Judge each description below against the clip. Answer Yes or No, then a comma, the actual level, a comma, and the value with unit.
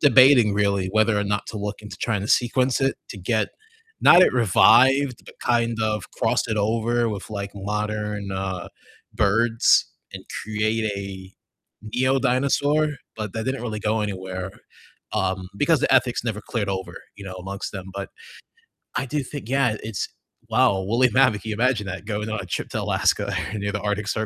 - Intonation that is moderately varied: Yes, average, 3.4 semitones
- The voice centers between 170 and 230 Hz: No, low, 110 Hz